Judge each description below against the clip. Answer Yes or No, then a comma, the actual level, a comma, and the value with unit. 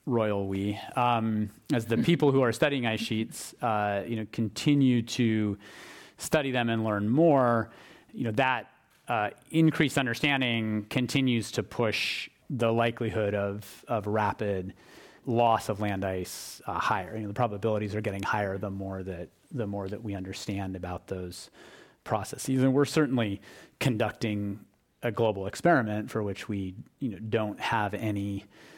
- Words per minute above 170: No, average, 155 wpm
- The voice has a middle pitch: No, low, 110 Hz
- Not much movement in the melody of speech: No, average, 3.2 semitones